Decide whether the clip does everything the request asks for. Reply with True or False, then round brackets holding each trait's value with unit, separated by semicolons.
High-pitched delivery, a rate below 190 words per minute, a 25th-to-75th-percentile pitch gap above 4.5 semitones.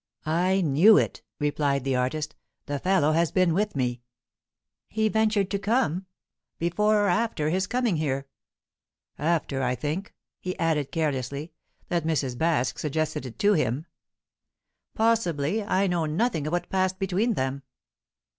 False (165 Hz; 145 wpm; 5.2 semitones)